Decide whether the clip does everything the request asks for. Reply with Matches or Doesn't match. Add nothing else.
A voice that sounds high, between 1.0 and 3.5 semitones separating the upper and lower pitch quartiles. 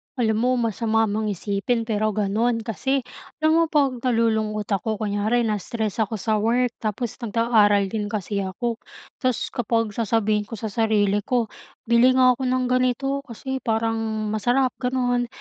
Matches